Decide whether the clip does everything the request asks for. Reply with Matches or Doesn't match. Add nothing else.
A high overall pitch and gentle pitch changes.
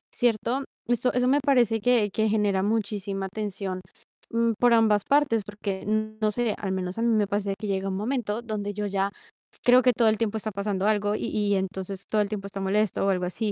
Matches